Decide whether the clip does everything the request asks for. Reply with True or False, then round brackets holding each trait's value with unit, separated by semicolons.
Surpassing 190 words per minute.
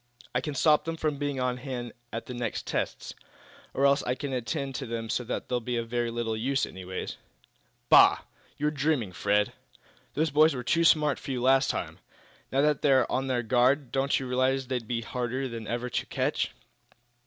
True (200 wpm)